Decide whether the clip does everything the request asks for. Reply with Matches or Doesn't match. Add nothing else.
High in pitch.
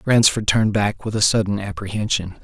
Doesn't match